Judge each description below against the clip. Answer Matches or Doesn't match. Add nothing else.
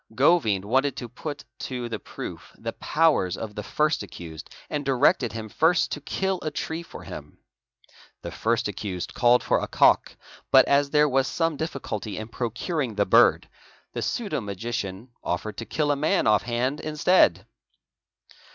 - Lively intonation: Matches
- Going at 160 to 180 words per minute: Matches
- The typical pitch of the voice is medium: Doesn't match